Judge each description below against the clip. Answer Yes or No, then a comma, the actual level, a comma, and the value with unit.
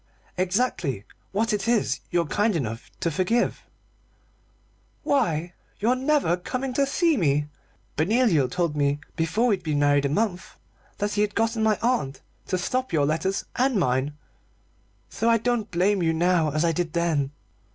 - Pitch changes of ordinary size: No, wide, 6.7 semitones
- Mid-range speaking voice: Yes, medium, 180 Hz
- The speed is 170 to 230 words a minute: No, average, 160 wpm